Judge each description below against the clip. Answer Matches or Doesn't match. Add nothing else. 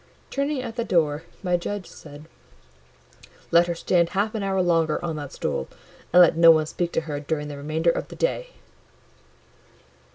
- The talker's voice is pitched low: Doesn't match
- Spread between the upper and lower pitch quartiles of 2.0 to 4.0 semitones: Matches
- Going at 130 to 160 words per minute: Doesn't match